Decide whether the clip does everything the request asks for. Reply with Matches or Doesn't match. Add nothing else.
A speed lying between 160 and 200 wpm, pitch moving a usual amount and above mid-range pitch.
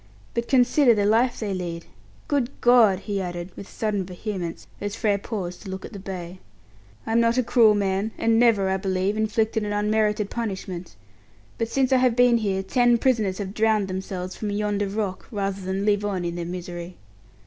Matches